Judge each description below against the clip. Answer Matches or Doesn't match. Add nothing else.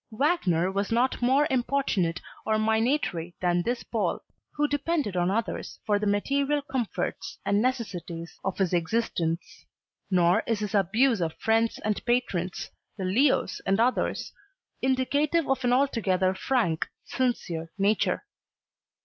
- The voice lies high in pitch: Matches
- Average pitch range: Doesn't match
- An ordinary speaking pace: Doesn't match